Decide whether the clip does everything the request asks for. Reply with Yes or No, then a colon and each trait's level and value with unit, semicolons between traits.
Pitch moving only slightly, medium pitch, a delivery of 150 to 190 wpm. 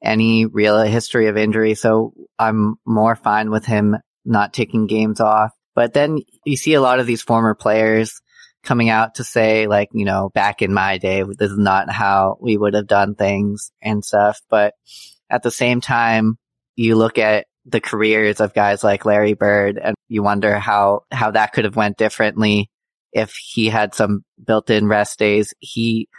No: narrow, 1.4 semitones; low, 110 Hz; average, 185 wpm